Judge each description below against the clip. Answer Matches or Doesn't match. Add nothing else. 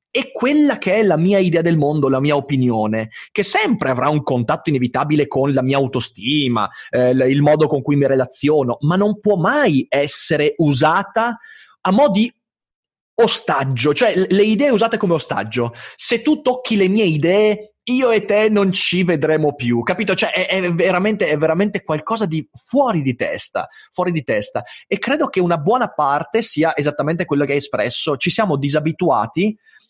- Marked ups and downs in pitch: Matches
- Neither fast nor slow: Doesn't match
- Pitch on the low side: Doesn't match